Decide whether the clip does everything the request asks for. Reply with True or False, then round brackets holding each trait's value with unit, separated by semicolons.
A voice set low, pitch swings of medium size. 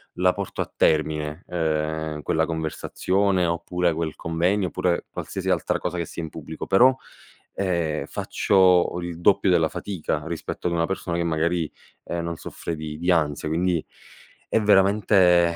False (85 Hz; 2.3 semitones)